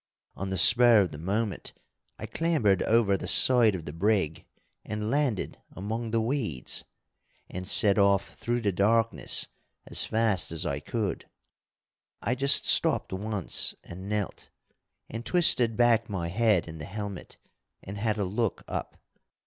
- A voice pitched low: Yes, low, 105 Hz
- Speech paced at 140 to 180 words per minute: Yes, average, 150 wpm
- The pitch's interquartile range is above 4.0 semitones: No, average, 3.3 semitones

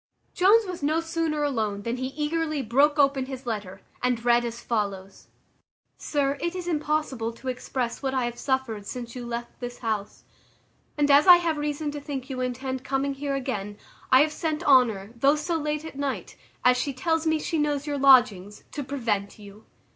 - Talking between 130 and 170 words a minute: No, average, 190 wpm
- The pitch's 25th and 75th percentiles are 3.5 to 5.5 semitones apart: Yes, average, 4.0 semitones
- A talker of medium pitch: No, very high, 270 Hz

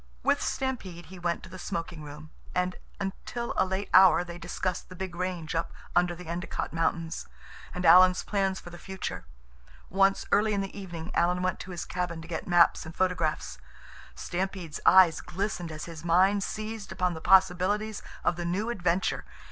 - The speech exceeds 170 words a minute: Yes, average, 180 wpm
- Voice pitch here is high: No, medium, 180 Hz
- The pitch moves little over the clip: Yes, narrow, 2.0 semitones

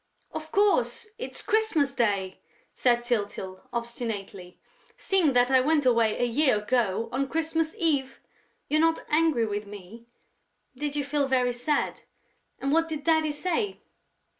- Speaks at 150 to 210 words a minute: No, average, 140 wpm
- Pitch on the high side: Yes, very high, 265 Hz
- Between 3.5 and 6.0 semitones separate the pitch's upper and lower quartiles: Yes, average, 5.3 semitones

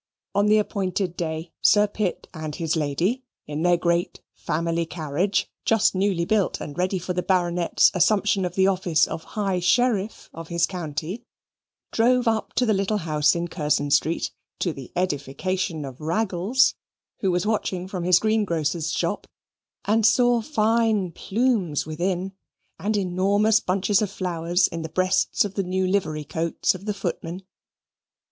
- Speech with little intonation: No, average, 3.6 semitones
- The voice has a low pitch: No, medium, 185 Hz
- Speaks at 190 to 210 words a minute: No, average, 155 wpm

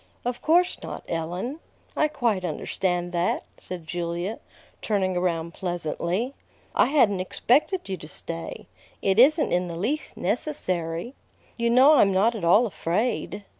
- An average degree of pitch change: No, wide, 5.9 semitones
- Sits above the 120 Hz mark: Yes, high, 190 Hz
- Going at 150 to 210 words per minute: No, average, 140 wpm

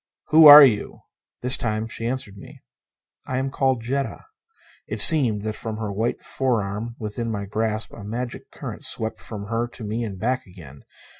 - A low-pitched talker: Yes, low, 115 Hz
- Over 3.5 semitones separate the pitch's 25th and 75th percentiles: No, average, 3.2 semitones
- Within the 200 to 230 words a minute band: No, average, 175 wpm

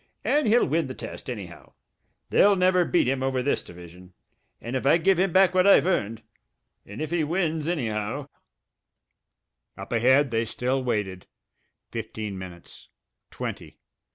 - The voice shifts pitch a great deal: Yes, wide, 8.0 semitones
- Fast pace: No, average, 150 wpm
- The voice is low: Yes, low, 130 Hz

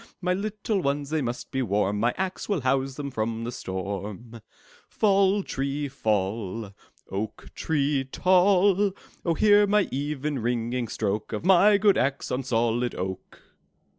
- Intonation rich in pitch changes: Yes, wide, 8.3 semitones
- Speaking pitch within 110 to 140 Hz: Yes, low, 135 Hz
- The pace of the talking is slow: No, average, 145 wpm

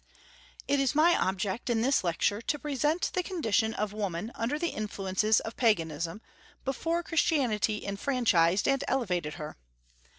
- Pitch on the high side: Yes, high, 225 Hz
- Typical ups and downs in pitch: No, wide, 6.3 semitones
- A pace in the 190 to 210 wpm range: No, average, 140 wpm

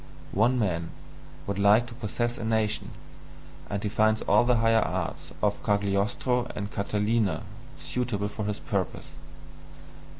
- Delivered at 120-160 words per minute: Yes, slow, 135 wpm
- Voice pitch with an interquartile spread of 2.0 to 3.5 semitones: Yes, narrow, 2.4 semitones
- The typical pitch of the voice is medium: No, low, 105 Hz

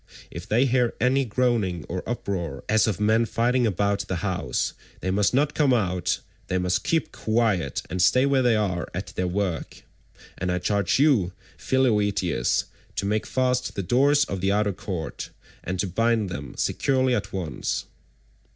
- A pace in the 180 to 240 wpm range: No, average, 170 wpm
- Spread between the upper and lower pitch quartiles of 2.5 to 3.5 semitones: No, average, 5.1 semitones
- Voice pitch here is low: Yes, low, 105 Hz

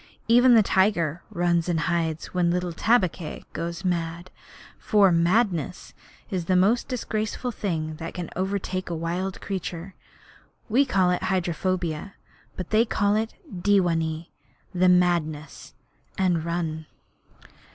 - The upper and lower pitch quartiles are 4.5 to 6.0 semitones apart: No, average, 2.7 semitones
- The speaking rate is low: Yes, slow, 125 wpm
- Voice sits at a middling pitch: Yes, medium, 180 Hz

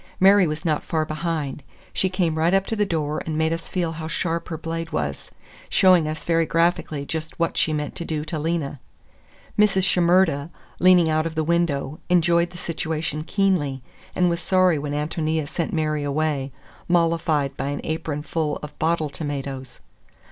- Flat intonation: Yes, narrow, 2.2 semitones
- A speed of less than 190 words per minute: Yes, average, 175 wpm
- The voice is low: No, medium, 160 Hz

